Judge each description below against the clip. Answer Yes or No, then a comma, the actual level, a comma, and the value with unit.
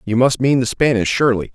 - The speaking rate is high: Yes, fast, 235 wpm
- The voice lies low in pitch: Yes, low, 120 Hz